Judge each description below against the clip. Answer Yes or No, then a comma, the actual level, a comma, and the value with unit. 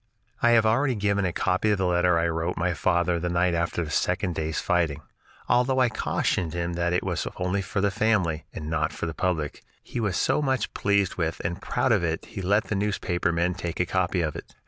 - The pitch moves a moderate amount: Yes, average, 3.0 semitones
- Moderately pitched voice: No, very low, 90 Hz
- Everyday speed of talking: No, fast, 235 wpm